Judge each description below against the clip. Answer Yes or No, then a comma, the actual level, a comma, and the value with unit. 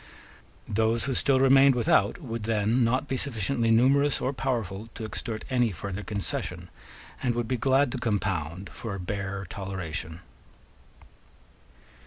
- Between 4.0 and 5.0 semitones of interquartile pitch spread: Yes, average, 4.6 semitones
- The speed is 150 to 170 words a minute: No, average, 140 wpm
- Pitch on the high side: No, low, 115 Hz